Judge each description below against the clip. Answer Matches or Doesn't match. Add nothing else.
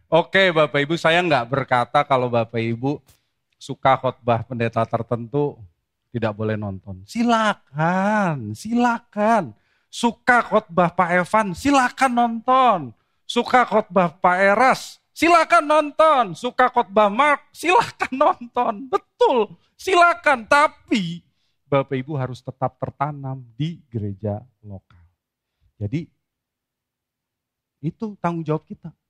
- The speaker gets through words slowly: Doesn't match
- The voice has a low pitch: Doesn't match